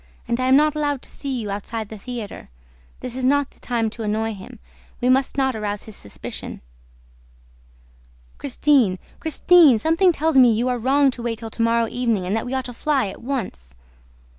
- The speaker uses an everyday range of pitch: Yes, average, 3.7 semitones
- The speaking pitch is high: Yes, high, 245 Hz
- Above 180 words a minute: Yes, average, 200 wpm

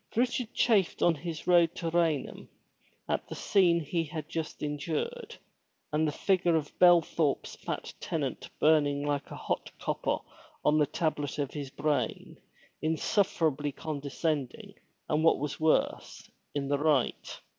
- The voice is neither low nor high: Yes, medium, 155 Hz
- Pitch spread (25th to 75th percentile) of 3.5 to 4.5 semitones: No, average, 2.7 semitones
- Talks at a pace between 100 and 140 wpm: Yes, slow, 135 wpm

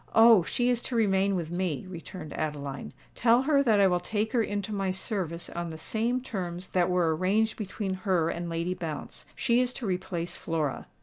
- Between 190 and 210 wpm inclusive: Yes, average, 195 wpm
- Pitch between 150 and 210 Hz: Yes, high, 190 Hz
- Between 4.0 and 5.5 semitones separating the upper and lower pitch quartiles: Yes, average, 4.5 semitones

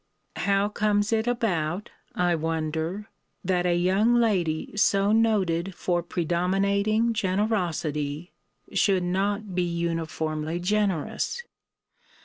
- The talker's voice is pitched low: No, medium, 185 Hz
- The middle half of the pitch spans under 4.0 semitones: Yes, average, 3.5 semitones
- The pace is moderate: No, slow, 100 wpm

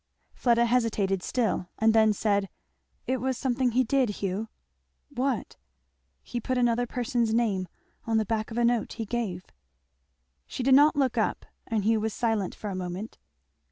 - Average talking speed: Yes, average, 165 wpm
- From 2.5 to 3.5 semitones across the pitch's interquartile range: Yes, average, 2.8 semitones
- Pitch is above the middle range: Yes, high, 230 Hz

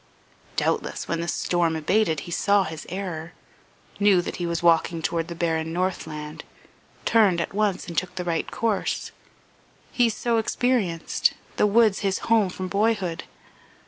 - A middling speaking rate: Yes, average, 150 wpm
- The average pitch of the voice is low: No, medium, 180 Hz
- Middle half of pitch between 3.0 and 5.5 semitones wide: Yes, average, 3.8 semitones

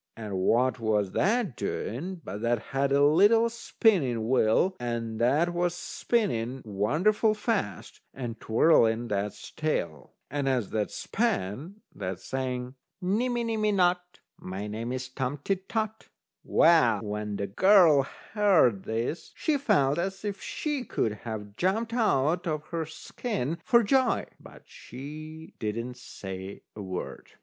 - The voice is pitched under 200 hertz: Yes, medium, 140 Hz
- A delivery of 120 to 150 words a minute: Yes, slow, 135 wpm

